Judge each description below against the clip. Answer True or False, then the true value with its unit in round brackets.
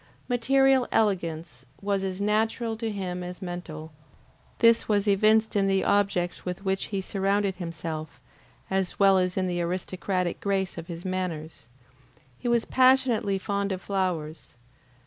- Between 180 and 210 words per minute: False (145 wpm)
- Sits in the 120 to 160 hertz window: False (190 Hz)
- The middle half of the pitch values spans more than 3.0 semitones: False (2.7 semitones)